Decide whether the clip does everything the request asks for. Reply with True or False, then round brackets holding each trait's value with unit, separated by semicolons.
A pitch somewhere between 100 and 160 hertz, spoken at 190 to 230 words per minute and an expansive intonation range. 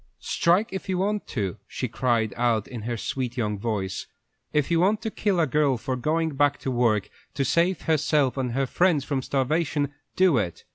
True (135 Hz; 195 wpm; 5.7 semitones)